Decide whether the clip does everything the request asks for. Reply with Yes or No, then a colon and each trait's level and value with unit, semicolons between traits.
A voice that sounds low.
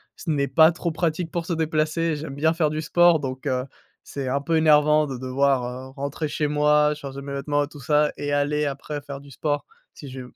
No: medium, 150 Hz